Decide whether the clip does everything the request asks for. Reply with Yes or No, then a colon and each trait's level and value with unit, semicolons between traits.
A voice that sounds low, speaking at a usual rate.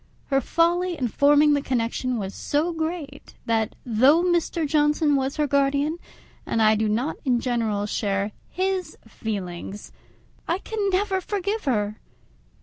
No: very high, 280 Hz; average, 145 wpm